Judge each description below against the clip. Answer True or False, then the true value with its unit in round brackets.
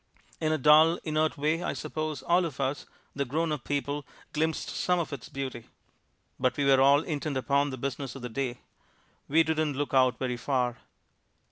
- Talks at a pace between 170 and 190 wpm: True (180 wpm)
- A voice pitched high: False (145 Hz)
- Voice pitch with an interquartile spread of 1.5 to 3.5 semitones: True (2.8 semitones)